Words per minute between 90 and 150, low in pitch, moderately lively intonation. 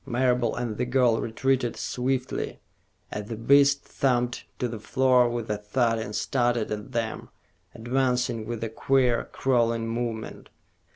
No: average, 140 wpm; low, 120 Hz; narrow, 2.0 semitones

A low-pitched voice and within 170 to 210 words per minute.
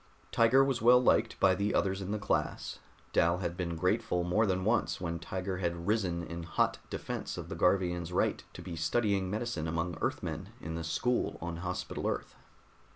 Yes: very low, 90 Hz; average, 185 wpm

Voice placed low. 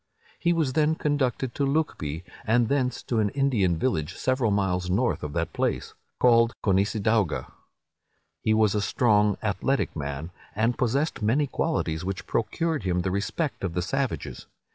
Yes: low, 110 Hz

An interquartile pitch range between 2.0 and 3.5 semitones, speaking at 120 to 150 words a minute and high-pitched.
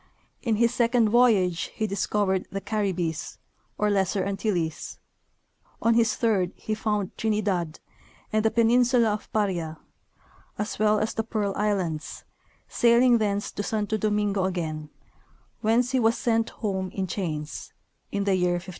Yes: average, 2.9 semitones; average, 145 wpm; high, 210 Hz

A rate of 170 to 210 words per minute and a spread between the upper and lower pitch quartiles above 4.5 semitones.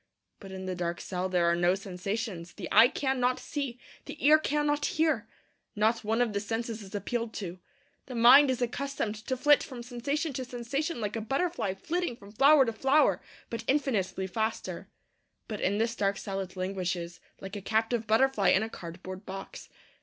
Yes: average, 185 wpm; wide, 5.4 semitones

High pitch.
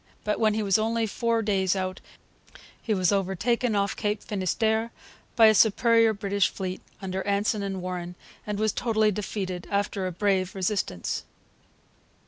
Yes: high, 205 Hz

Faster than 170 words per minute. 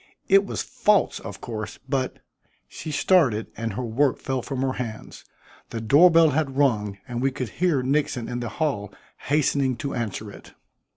Yes: average, 180 wpm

